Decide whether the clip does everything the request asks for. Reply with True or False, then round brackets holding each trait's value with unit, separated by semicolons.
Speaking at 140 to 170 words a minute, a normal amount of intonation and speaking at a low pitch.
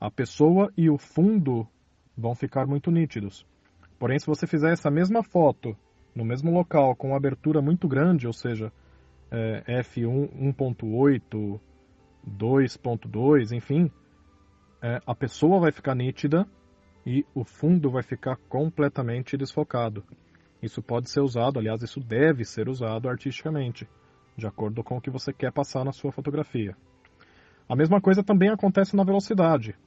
True (145 wpm; 4.8 semitones; 130 Hz)